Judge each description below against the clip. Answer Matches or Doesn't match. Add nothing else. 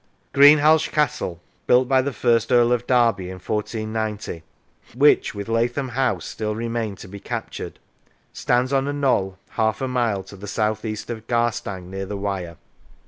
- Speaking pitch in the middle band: Doesn't match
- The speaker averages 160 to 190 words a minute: Matches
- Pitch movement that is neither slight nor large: Matches